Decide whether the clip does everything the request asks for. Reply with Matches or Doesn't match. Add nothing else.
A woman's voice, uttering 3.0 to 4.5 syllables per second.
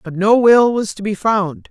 Matches